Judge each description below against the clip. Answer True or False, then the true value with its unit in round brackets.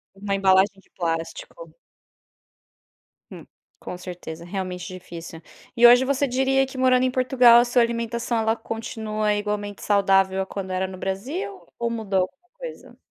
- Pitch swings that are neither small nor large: True (4.7 semitones)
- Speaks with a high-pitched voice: True (215 Hz)